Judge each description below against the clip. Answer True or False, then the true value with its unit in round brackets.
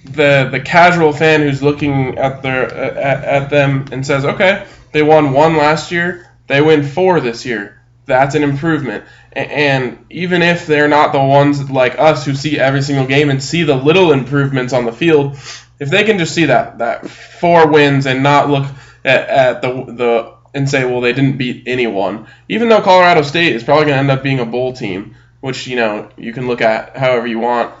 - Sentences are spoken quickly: True (210 wpm)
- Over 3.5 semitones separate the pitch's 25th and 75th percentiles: False (3.2 semitones)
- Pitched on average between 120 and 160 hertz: True (140 Hz)